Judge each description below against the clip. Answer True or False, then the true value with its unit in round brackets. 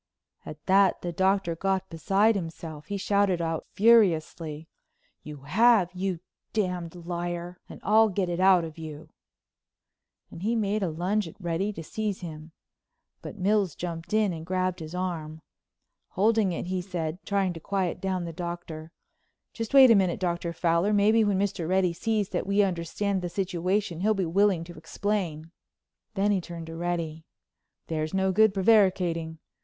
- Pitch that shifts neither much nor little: True (3.2 semitones)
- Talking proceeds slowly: False (165 wpm)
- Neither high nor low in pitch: True (180 Hz)